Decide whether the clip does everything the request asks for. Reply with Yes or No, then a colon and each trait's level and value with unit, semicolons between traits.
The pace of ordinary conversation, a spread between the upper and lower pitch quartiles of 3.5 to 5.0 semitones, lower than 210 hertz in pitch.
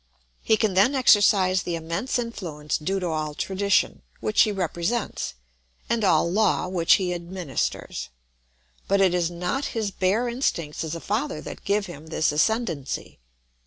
Yes: average, 155 wpm; average, 4.2 semitones; medium, 185 Hz